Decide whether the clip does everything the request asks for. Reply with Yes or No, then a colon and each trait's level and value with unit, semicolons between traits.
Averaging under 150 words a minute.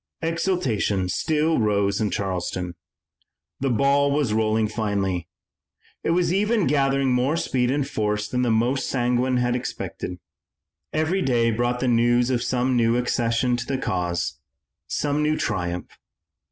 Yes: average, 140 wpm